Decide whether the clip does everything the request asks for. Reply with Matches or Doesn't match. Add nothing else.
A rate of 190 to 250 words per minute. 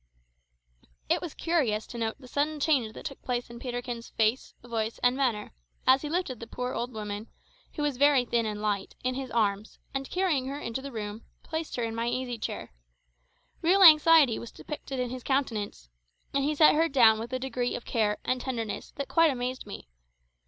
Matches